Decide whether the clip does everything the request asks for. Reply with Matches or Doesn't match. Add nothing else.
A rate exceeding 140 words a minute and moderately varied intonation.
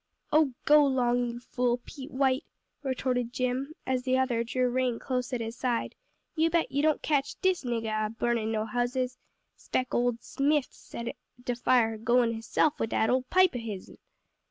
Doesn't match